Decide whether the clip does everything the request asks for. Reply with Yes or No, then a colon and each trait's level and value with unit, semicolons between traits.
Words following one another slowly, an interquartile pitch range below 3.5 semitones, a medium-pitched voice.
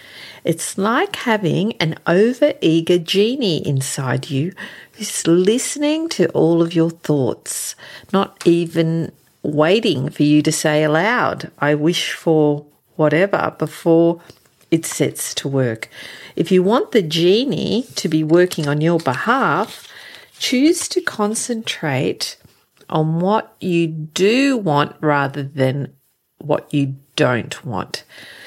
No: slow, 120 wpm; average, 5.3 semitones; medium, 165 Hz